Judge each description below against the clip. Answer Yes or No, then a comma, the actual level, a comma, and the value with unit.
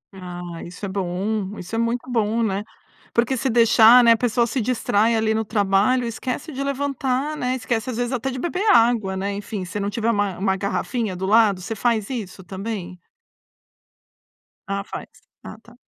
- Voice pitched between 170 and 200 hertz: No, high, 220 Hz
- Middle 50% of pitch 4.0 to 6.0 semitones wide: No, average, 3.6 semitones